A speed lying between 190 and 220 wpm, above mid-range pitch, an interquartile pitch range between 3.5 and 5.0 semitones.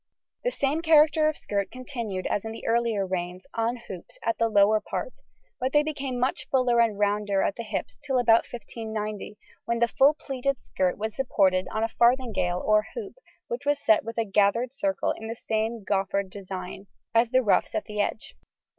Yes: average, 195 wpm; high, 225 Hz; average, 4.0 semitones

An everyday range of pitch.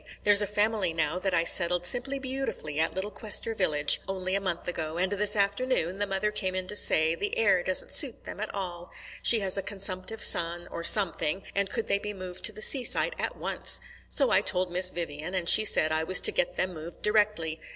Yes: average, 3.4 semitones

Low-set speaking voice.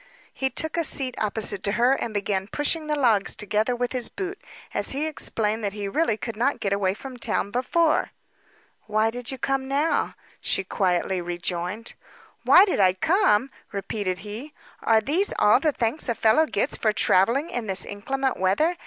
No: high, 230 Hz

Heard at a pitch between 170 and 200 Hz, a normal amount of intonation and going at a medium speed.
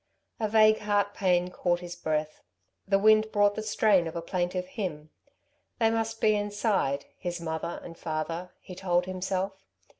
Yes: medium, 185 Hz; average, 3.1 semitones; average, 160 wpm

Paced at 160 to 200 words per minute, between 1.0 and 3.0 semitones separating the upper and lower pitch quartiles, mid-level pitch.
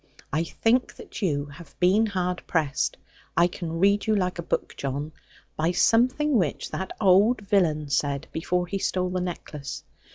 No: average, 165 wpm; average, 4.3 semitones; medium, 180 Hz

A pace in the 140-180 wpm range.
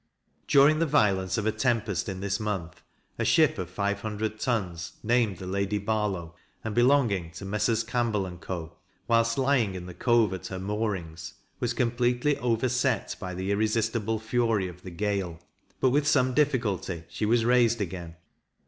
Yes: average, 165 wpm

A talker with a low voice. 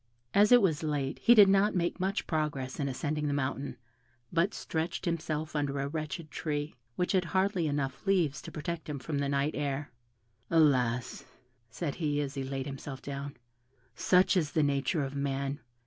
No: medium, 150 Hz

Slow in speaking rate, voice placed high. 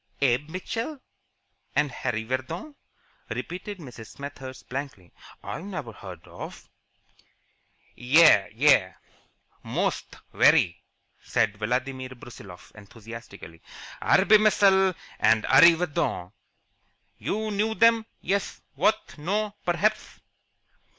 No: slow, 90 wpm; medium, 140 Hz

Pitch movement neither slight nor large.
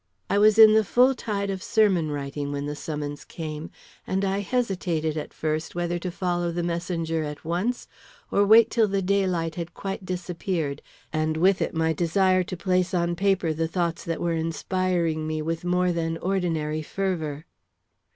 Yes: average, 3.2 semitones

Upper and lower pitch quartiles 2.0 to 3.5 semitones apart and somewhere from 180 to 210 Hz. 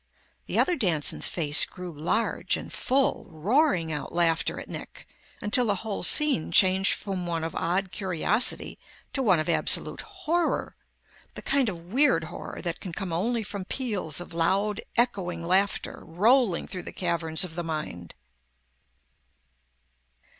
No: average, 5.0 semitones; medium, 185 Hz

